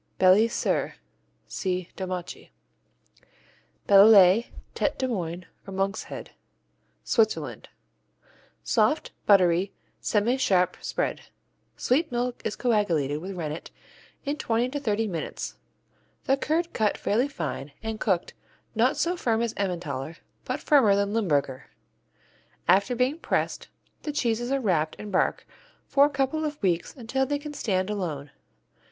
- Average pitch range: No, wide, 5.7 semitones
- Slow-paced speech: Yes, slow, 130 wpm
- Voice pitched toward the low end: No, high, 210 Hz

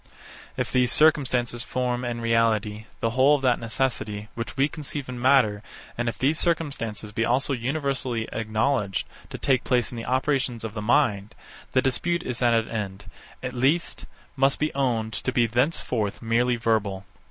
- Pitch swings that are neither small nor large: Yes, average, 3.0 semitones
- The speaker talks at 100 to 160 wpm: No, average, 170 wpm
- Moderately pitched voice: No, low, 120 Hz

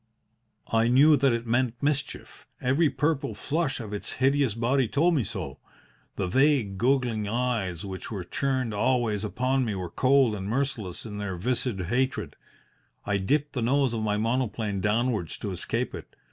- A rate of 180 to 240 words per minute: No, average, 165 wpm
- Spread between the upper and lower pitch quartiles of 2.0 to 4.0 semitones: No, average, 4.5 semitones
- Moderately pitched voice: No, low, 120 Hz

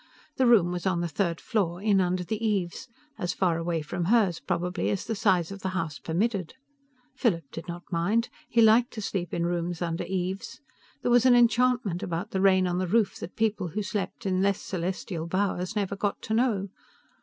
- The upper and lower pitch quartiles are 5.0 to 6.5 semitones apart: No, average, 3.4 semitones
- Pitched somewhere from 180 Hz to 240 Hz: Yes, high, 190 Hz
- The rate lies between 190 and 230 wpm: Yes, average, 200 wpm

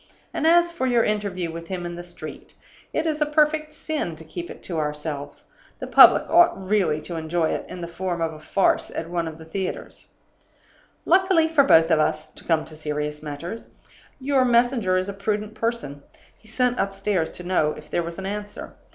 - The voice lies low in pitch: No, medium, 185 Hz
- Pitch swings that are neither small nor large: No, wide, 7.0 semitones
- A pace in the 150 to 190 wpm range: No, fast, 205 wpm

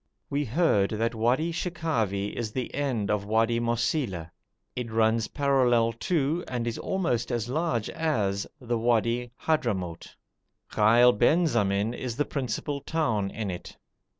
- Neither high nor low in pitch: No, low, 120 Hz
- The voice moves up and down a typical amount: Yes, average, 4.4 semitones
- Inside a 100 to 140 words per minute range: Yes, slow, 135 wpm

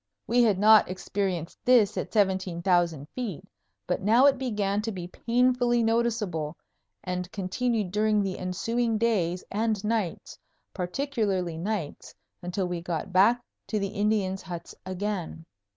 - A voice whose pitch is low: No, high, 200 Hz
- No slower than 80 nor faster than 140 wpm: Yes, slow, 135 wpm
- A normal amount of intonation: Yes, average, 3.9 semitones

